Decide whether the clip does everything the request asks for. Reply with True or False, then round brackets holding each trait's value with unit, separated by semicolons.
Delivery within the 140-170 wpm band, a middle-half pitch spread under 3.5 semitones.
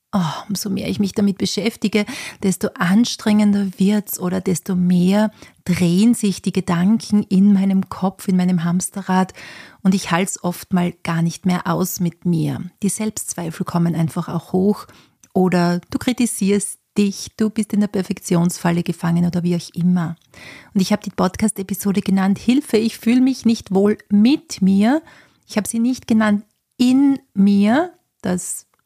True (160 wpm; 3.1 semitones)